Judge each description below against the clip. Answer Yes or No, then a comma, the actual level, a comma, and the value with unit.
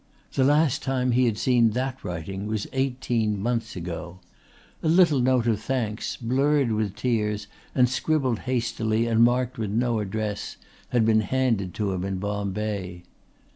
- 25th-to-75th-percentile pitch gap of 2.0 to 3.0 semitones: No, average, 3.6 semitones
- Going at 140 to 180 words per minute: Yes, average, 155 wpm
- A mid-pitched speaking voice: No, low, 115 Hz